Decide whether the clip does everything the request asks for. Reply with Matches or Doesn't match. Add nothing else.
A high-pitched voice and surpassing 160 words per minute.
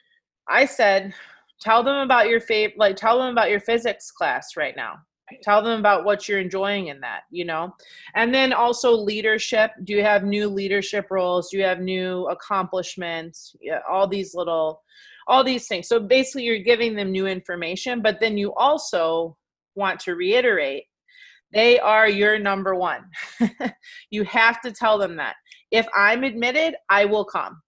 Matches